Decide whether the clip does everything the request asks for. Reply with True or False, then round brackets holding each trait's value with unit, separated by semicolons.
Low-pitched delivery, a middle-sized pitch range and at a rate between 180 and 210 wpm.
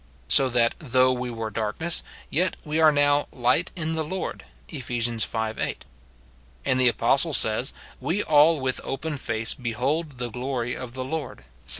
True (130 Hz; 4.3 semitones; 185 wpm)